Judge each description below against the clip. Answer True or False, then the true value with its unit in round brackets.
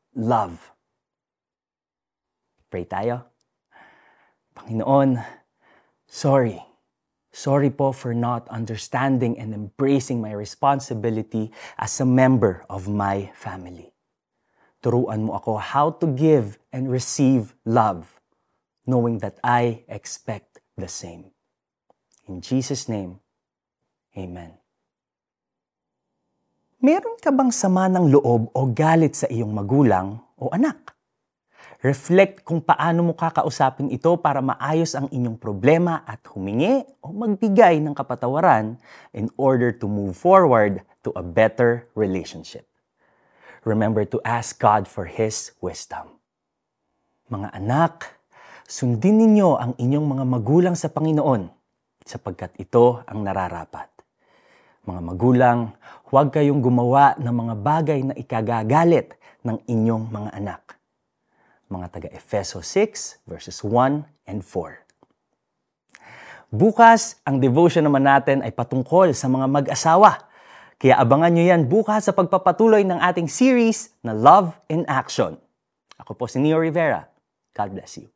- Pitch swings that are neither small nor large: False (6.1 semitones)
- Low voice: True (130 Hz)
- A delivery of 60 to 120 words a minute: True (115 wpm)